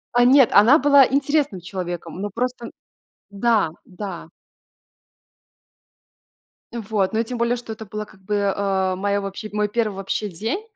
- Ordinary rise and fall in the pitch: Yes, average, 3.6 semitones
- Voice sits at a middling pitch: No, high, 210 Hz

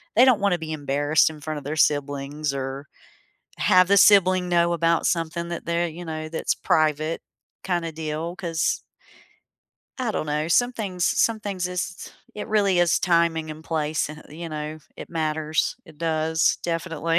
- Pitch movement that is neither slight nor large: No, narrow, 2.3 semitones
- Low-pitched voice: No, medium, 165 Hz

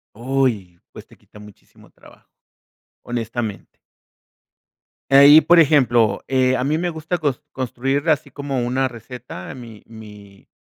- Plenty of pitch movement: No, average, 4.2 semitones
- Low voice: Yes, low, 130 Hz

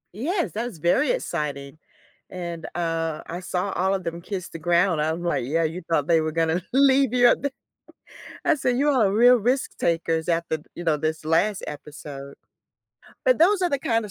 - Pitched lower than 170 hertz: No, medium, 175 Hz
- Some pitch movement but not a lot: No, wide, 7.1 semitones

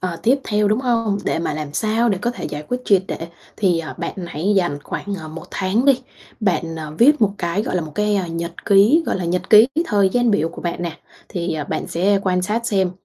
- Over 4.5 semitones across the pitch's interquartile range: No, average, 4.1 semitones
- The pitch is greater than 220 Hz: No, high, 190 Hz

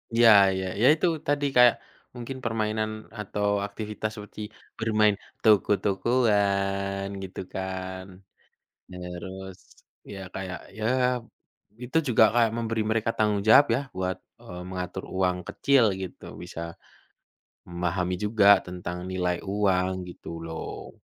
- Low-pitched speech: Yes, low, 100 Hz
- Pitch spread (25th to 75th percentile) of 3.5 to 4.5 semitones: No, average, 3.1 semitones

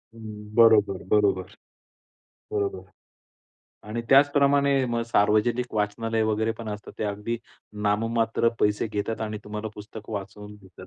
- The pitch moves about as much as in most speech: No, narrow, 2.0 semitones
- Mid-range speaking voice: No, low, 110 Hz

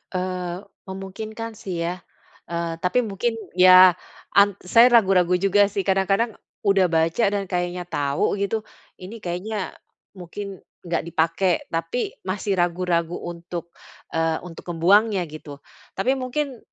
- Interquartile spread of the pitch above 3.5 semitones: No, average, 2.7 semitones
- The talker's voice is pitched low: No, medium, 185 Hz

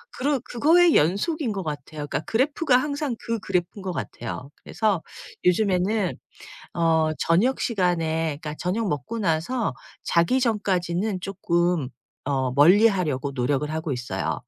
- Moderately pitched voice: Yes, medium, 180 Hz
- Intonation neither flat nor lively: No, wide, 6.2 semitones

